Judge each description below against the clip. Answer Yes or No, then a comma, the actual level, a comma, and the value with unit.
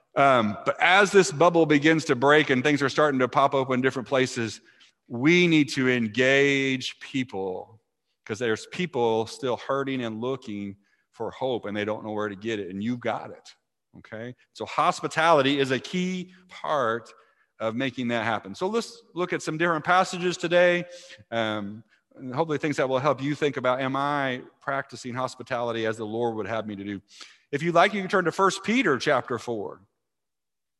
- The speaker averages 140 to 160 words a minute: No, average, 185 wpm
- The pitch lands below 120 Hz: No, low, 135 Hz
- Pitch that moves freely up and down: Yes, wide, 6.2 semitones